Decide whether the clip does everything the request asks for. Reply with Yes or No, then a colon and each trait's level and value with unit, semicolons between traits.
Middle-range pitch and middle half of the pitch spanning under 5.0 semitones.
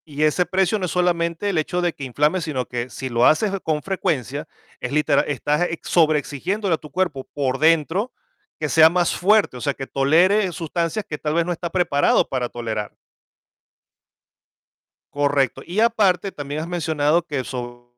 Yes: medium, 160 Hz; average, 4.0 semitones